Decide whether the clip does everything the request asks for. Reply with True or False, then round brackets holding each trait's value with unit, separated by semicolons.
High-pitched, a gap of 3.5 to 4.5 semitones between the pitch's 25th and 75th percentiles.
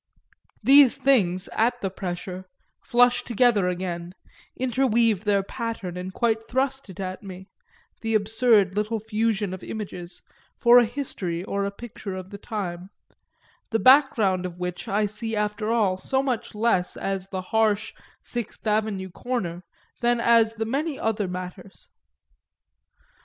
True (210 Hz; 3.8 semitones)